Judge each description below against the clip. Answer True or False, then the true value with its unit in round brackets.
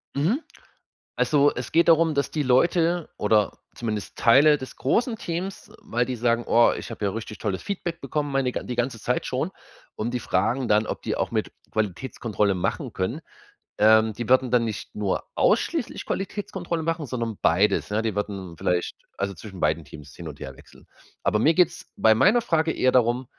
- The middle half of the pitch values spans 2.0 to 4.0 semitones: False (6.5 semitones)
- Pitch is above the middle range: False (120 Hz)